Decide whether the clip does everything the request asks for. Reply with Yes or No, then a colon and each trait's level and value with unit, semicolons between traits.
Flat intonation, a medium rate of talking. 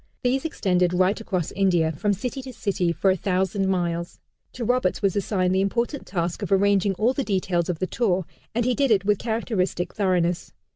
No: average, 3.6 semitones; average, 195 wpm